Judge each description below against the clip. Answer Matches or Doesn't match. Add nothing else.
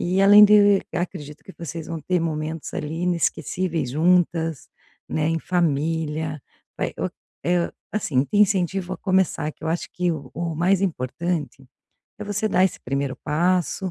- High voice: Doesn't match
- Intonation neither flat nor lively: Matches